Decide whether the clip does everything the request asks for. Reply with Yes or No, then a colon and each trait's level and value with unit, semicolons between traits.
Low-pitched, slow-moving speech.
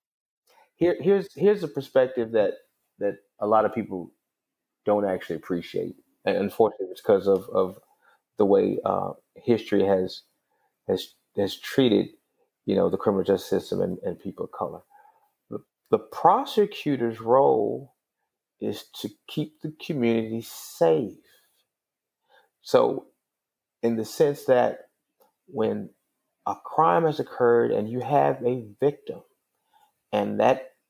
Yes: low, 130 Hz; slow, 125 wpm